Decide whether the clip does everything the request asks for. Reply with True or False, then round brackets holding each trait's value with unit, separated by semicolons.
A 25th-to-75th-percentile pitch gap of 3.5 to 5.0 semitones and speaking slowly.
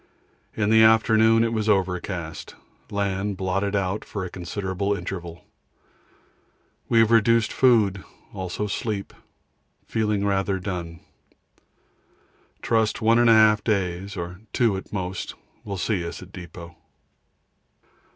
False (3.0 semitones; 115 wpm)